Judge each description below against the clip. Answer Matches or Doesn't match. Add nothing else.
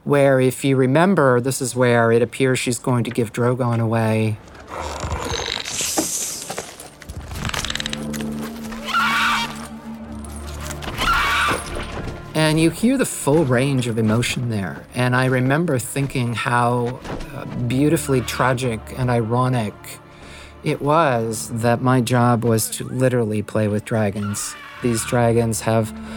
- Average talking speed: Doesn't match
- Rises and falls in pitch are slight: Doesn't match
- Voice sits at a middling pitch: Doesn't match